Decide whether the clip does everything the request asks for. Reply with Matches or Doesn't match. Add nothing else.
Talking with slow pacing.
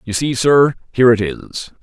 Doesn't match